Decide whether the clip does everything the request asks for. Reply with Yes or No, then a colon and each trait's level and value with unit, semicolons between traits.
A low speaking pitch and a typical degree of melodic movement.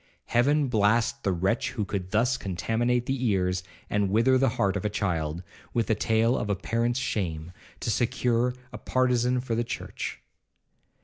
Yes: low, 115 Hz; average, 3.8 semitones